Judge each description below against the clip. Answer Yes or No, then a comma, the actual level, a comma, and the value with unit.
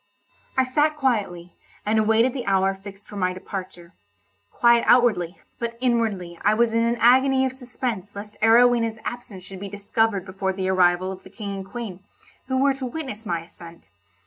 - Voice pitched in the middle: No, high, 210 Hz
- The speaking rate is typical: Yes, average, 170 wpm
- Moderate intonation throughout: Yes, average, 4.3 semitones